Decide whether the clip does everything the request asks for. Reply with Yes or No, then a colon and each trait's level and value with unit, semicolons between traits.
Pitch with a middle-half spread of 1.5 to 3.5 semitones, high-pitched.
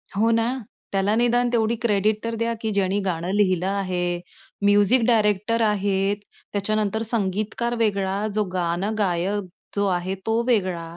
Yes: average, 2.7 semitones; high, 205 Hz